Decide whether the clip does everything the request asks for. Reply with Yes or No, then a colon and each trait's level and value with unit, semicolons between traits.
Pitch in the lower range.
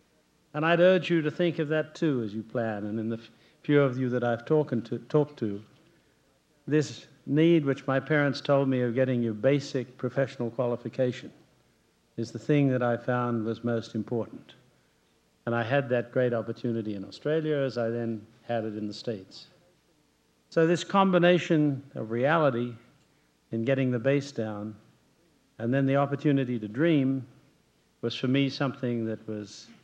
Yes: low, 130 Hz